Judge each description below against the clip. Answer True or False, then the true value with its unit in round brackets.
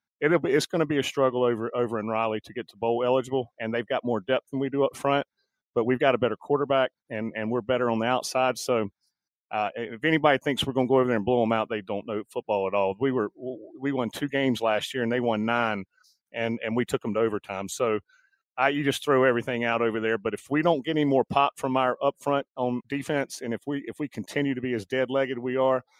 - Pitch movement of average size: True (3.1 semitones)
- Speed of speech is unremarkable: False (270 wpm)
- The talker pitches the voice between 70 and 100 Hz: False (125 Hz)